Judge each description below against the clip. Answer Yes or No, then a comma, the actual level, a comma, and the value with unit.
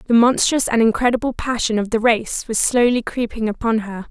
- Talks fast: No, average, 190 wpm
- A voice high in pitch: Yes, high, 230 Hz